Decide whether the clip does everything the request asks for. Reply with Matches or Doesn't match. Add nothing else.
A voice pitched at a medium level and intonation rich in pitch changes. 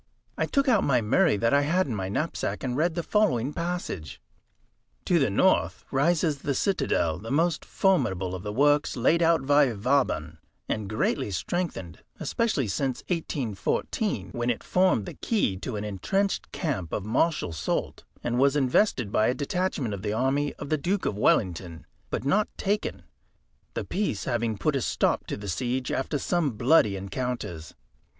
Doesn't match